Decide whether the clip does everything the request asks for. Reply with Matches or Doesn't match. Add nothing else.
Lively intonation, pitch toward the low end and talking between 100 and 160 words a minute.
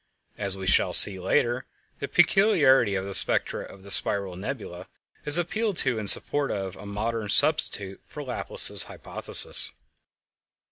Matches